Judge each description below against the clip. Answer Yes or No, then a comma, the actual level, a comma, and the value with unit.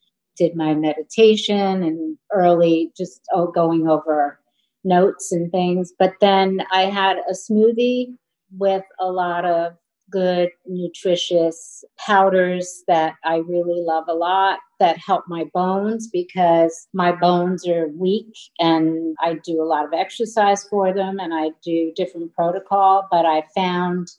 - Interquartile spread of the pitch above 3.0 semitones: No, narrow, 2.6 semitones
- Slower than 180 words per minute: Yes, average, 140 wpm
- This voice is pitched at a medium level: Yes, medium, 180 Hz